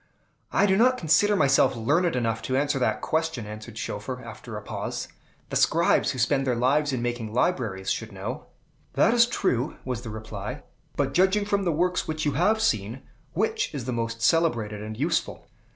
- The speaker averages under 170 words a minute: No, average, 185 wpm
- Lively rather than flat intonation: Yes, wide, 6.7 semitones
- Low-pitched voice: Yes, low, 130 Hz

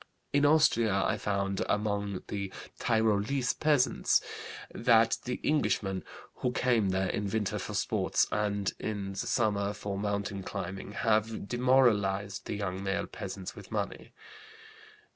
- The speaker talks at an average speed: No, slow, 130 wpm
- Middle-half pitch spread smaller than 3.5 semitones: Yes, average, 2.8 semitones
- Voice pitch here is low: Yes, low, 105 Hz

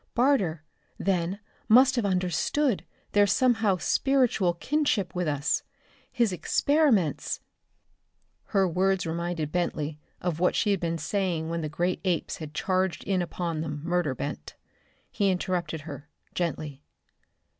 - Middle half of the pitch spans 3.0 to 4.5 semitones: Yes, average, 3.7 semitones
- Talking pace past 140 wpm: No, slow, 135 wpm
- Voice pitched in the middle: Yes, medium, 180 Hz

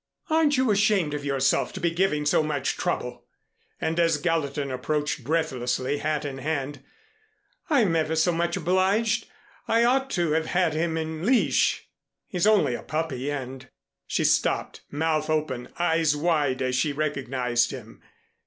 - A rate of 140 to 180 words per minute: Yes, average, 155 wpm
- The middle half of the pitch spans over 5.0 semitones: No, average, 3.7 semitones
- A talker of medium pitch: Yes, medium, 155 Hz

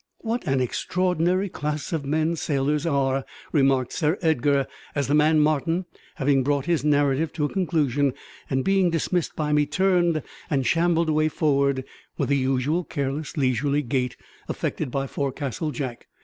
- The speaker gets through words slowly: No, average, 155 wpm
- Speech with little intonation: No, average, 3.1 semitones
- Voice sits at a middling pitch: Yes, medium, 150 Hz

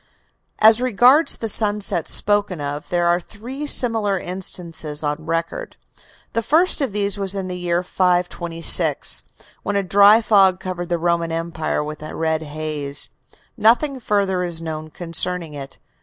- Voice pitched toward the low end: No, medium, 180 Hz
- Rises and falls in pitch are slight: No, average, 4.1 semitones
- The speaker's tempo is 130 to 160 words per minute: Yes, average, 150 wpm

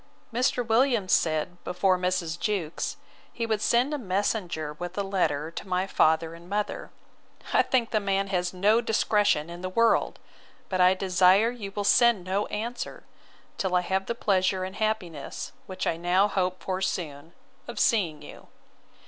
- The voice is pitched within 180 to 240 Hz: Yes, high, 190 Hz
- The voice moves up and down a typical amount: Yes, average, 3.2 semitones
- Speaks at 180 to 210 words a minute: No, average, 165 wpm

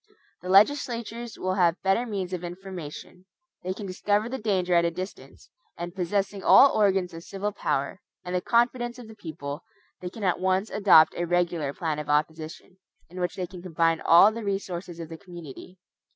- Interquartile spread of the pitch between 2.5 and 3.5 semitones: Yes, average, 3.1 semitones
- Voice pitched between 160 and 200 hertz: Yes, medium, 185 Hz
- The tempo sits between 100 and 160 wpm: No, average, 190 wpm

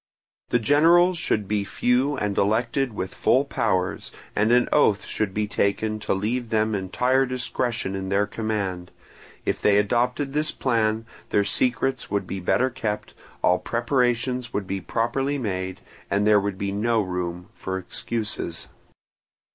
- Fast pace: No, average, 150 wpm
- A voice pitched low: Yes, low, 110 Hz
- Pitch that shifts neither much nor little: Yes, average, 3.8 semitones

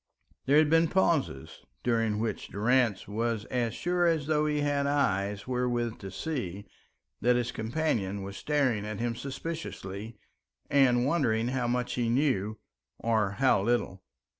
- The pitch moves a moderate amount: Yes, average, 4.8 semitones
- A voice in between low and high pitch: No, low, 120 Hz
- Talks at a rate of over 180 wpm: No, average, 145 wpm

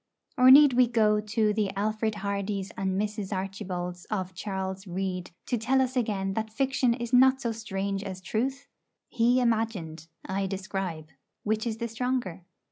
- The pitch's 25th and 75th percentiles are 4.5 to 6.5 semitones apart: No, average, 3.5 semitones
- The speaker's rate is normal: Yes, average, 160 wpm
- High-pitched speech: Yes, high, 210 Hz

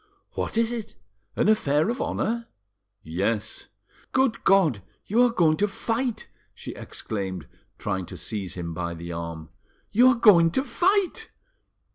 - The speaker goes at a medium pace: Yes, average, 145 wpm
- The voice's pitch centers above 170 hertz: Yes, high, 190 Hz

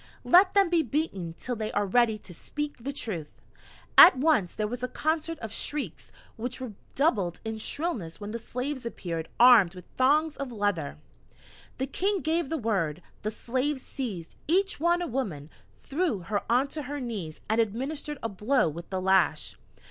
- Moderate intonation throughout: No, wide, 6.9 semitones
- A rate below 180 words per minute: Yes, average, 170 wpm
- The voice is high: Yes, high, 240 Hz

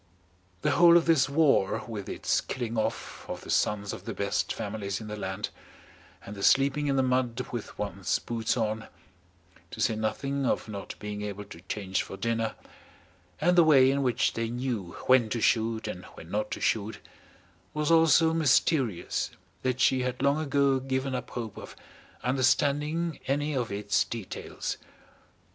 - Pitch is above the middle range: No, low, 125 Hz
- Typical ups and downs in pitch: Yes, average, 4.6 semitones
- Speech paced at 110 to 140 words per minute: No, average, 170 wpm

